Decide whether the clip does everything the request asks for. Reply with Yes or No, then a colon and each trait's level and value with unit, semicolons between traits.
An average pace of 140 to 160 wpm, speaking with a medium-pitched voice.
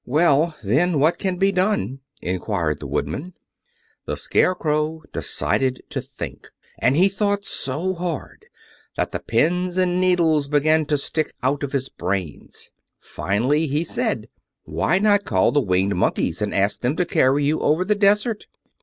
Yes: average, 155 wpm; medium, 155 Hz